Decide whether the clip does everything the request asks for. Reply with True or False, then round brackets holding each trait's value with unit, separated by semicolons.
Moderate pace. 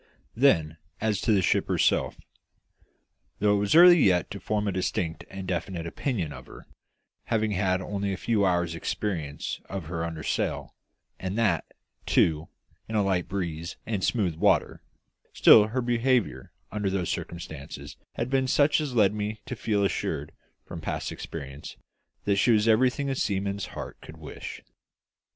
True (160 wpm)